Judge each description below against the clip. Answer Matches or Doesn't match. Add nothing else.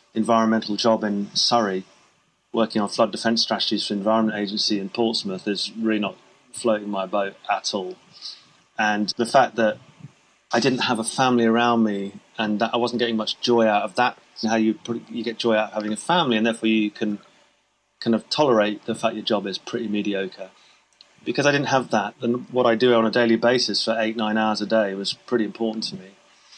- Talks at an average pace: Doesn't match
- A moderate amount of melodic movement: Doesn't match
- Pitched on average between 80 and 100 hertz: Doesn't match